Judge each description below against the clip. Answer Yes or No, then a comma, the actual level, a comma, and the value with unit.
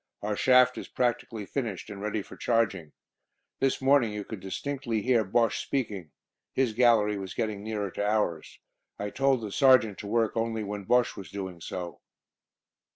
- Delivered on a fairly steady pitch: No, average, 3.3 semitones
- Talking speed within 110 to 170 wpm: Yes, average, 165 wpm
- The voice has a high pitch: No, low, 110 Hz